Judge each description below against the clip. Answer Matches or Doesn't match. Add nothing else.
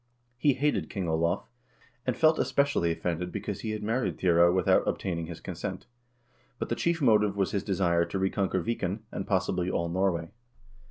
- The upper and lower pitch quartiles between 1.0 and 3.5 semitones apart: Doesn't match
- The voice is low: Matches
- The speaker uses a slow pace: Doesn't match